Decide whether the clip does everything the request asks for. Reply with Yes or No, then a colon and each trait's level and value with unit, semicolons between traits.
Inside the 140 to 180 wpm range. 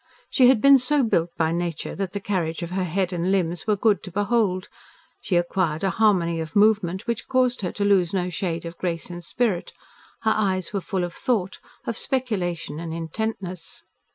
No: average, 195 wpm